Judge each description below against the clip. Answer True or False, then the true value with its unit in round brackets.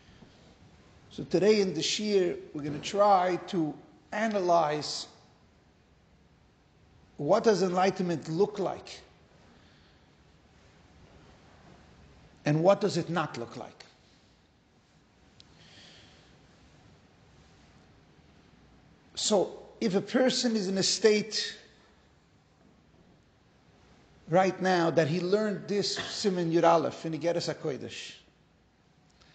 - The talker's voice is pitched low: False (170 Hz)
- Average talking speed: False (85 wpm)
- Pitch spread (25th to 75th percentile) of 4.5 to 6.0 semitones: True (5.5 semitones)